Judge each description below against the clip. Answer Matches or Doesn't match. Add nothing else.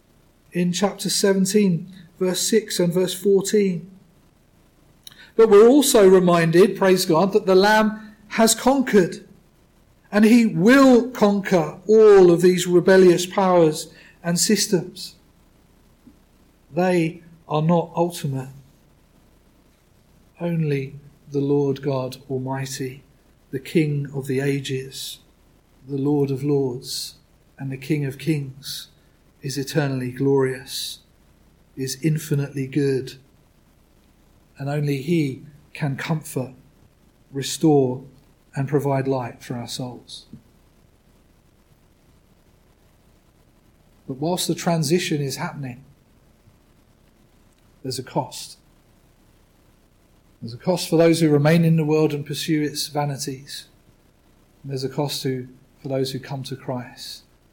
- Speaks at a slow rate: Matches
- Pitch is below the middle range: Doesn't match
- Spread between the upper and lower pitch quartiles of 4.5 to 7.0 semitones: Matches